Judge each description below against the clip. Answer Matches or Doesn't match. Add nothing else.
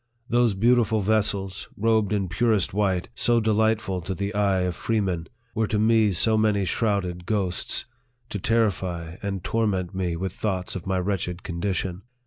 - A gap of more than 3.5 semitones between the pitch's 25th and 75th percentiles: Doesn't match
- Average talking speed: Matches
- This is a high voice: Doesn't match